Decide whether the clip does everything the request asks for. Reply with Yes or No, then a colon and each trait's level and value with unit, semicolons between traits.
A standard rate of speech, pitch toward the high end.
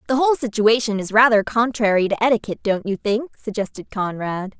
Yes: average, 170 wpm; high, 220 Hz